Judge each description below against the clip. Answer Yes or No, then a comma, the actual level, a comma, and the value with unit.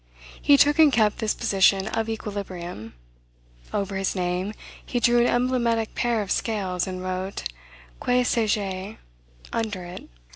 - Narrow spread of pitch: No, average, 3.9 semitones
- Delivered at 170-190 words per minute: No, average, 145 wpm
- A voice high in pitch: Yes, high, 210 Hz